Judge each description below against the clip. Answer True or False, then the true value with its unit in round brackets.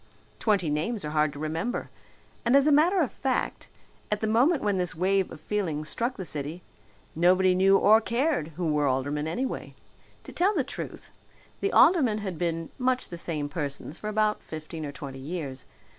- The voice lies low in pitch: False (185 Hz)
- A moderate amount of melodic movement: False (7.3 semitones)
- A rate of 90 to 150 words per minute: False (185 wpm)